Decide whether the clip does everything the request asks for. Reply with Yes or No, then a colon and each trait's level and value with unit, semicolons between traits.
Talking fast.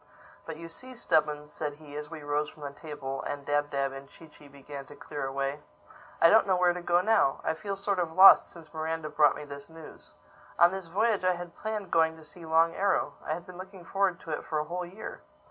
Yes: fast, 240 wpm